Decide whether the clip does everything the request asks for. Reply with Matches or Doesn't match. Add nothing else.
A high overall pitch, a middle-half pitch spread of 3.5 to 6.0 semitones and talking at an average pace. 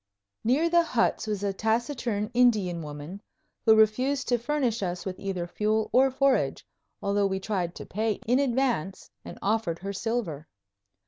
Matches